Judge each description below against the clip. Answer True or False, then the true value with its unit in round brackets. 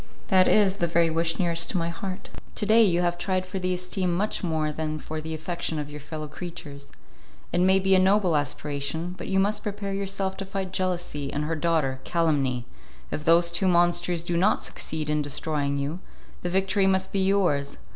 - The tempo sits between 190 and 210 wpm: True (200 wpm)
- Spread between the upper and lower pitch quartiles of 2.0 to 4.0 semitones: True (3.5 semitones)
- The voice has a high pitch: False (175 Hz)